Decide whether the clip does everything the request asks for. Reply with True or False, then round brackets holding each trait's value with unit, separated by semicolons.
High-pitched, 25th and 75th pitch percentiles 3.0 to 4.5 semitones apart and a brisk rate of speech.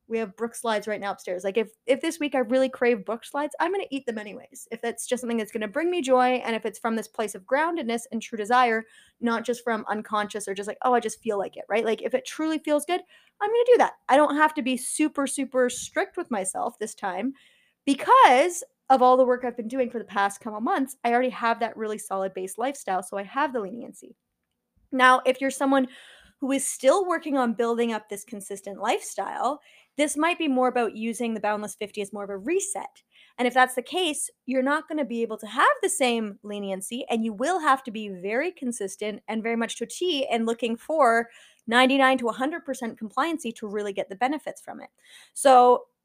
True (245 Hz; 3.9 semitones; 235 wpm)